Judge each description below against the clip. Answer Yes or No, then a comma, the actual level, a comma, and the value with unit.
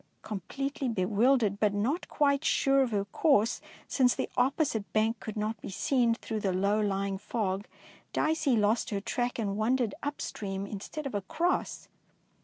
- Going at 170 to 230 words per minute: No, average, 160 wpm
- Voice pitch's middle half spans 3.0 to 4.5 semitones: No, average, 5.0 semitones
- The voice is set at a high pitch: Yes, high, 220 Hz